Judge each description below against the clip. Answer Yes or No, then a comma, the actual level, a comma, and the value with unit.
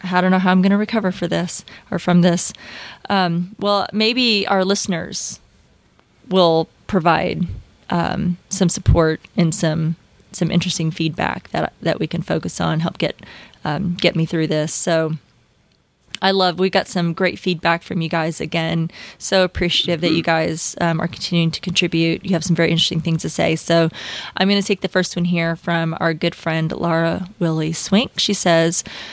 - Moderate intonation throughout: No, narrow, 2.2 semitones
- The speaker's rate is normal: Yes, average, 185 wpm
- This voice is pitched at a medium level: Yes, medium, 175 Hz